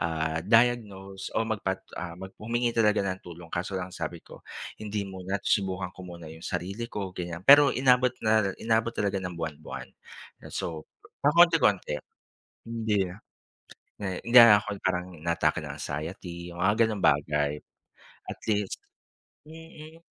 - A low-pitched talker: Yes, very low, 95 Hz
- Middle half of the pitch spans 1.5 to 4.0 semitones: No, average, 4.4 semitones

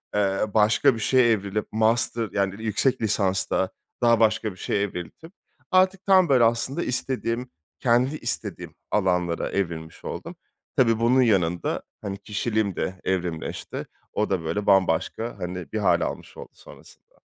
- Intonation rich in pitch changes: No, average, 3.9 semitones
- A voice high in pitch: No, low, 105 Hz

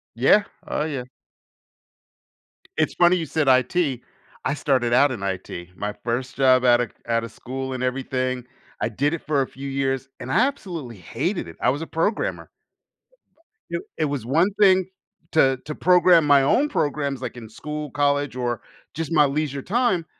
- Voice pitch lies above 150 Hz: No, low, 135 Hz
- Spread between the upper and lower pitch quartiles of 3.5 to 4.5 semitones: Yes, average, 3.9 semitones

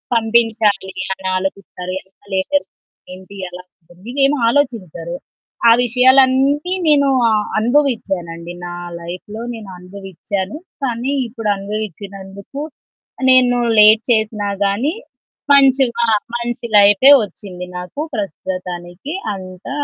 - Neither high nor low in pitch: No, high, 210 Hz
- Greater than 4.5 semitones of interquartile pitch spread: Yes, average, 4.9 semitones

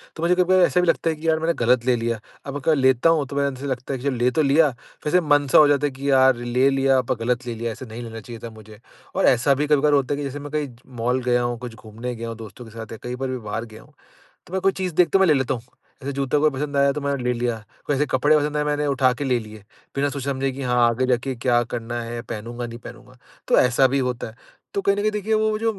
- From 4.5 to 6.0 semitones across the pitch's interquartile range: No, average, 3.5 semitones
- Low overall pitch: Yes, low, 130 Hz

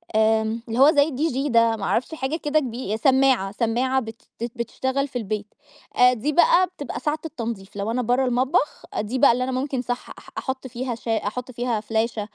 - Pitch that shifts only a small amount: No, average, 3.0 semitones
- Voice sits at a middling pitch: No, high, 245 Hz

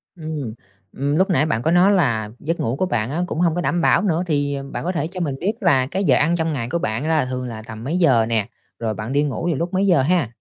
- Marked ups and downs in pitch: Yes, wide, 5.9 semitones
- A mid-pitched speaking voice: Yes, medium, 155 Hz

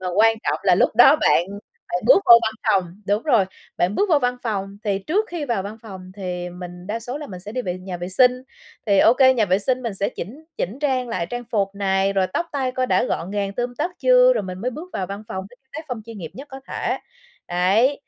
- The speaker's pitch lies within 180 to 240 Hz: Yes, high, 215 Hz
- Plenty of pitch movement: No, average, 5.0 semitones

